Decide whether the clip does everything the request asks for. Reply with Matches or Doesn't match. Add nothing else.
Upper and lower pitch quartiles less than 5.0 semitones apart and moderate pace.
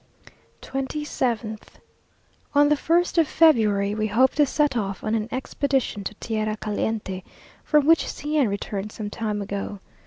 Doesn't match